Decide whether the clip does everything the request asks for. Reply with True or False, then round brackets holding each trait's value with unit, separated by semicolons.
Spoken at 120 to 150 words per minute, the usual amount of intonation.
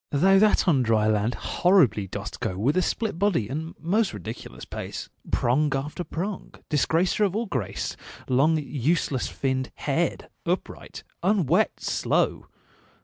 False (140 wpm; 6.7 semitones)